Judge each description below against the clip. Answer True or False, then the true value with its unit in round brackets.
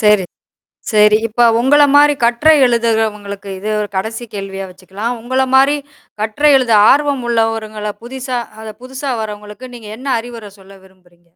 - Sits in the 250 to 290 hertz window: False (225 Hz)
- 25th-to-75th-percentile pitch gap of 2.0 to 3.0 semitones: False (3.6 semitones)